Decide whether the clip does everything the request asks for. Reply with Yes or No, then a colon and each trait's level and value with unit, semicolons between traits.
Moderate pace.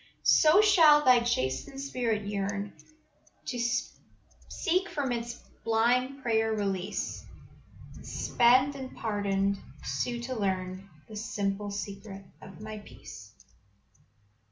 No: slow, 105 wpm